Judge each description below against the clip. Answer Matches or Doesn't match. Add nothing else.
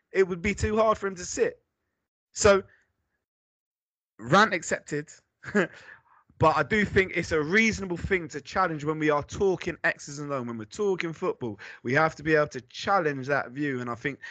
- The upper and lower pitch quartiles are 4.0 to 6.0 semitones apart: Matches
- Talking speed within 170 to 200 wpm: Matches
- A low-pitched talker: Doesn't match